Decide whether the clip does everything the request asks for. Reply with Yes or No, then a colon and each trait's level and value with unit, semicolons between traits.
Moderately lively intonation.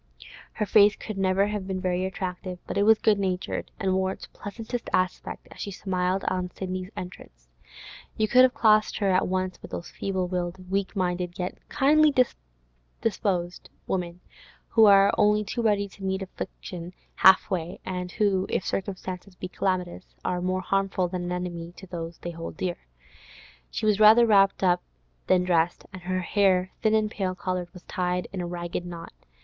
No: narrow, 1.8 semitones